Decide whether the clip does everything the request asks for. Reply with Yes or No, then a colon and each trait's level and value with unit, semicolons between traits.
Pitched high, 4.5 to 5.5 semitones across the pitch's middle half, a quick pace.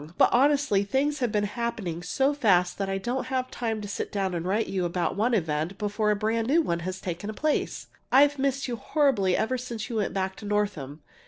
Yes: high, 210 Hz; average, 5.1 semitones; fast, 220 wpm